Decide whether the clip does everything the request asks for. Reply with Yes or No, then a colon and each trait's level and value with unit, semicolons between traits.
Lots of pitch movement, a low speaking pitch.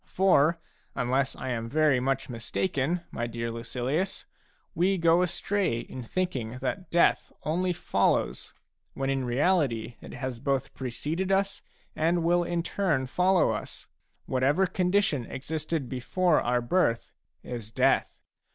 No: wide, 6.2 semitones; medium, 145 Hz